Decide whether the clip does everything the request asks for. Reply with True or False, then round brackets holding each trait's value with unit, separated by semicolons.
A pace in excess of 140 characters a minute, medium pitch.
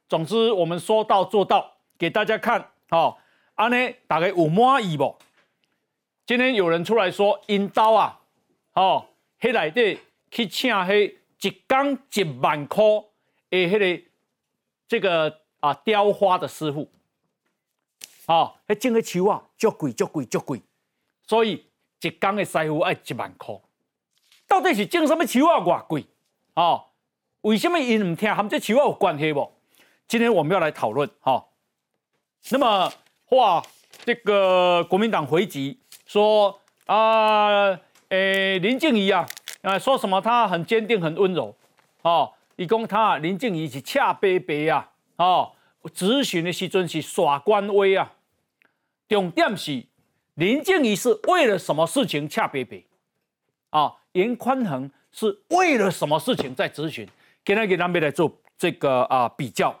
False (210 characters per minute; 205 Hz)